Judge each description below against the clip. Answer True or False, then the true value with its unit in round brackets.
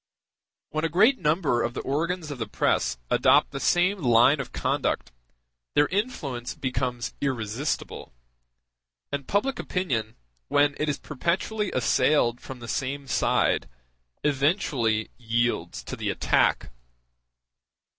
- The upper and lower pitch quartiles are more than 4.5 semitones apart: True (5.4 semitones)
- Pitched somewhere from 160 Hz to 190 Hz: False (140 Hz)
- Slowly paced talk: True (125 wpm)